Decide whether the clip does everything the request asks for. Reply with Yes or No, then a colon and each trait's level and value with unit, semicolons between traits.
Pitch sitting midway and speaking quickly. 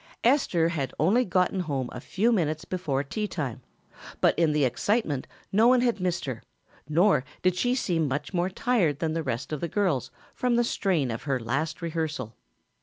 No: medium, 165 Hz; average, 185 wpm